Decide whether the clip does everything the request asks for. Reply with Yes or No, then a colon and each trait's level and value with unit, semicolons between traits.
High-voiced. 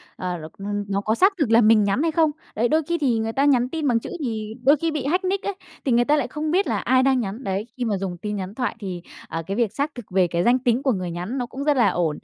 Yes: high, 240 Hz